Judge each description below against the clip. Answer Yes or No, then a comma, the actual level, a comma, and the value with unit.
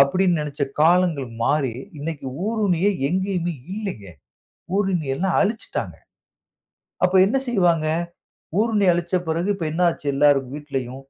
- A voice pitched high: No, medium, 170 Hz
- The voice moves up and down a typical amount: Yes, average, 4.7 semitones